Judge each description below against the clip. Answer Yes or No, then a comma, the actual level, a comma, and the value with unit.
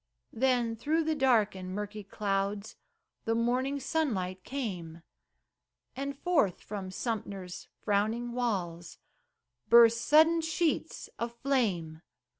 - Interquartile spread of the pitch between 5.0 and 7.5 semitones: Yes, wide, 5.4 semitones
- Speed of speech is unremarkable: No, slow, 105 wpm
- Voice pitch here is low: No, high, 225 Hz